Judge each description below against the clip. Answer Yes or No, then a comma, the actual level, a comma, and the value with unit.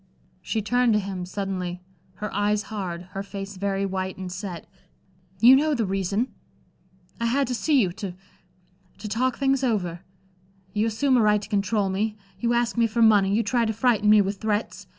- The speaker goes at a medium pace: Yes, average, 190 wpm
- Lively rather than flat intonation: No, average, 3.0 semitones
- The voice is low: No, high, 210 Hz